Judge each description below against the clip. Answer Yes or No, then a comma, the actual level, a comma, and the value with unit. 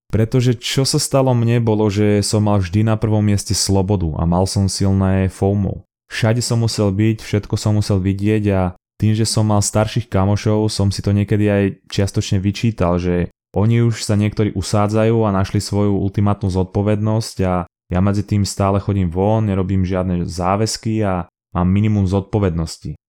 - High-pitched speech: No, low, 105 Hz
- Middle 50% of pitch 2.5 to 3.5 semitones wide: No, narrow, 2.1 semitones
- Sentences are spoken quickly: Yes, fast, 170 wpm